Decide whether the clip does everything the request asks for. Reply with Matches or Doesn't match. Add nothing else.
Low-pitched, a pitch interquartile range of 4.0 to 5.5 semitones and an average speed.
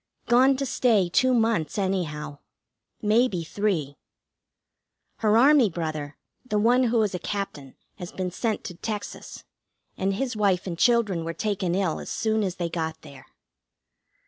Doesn't match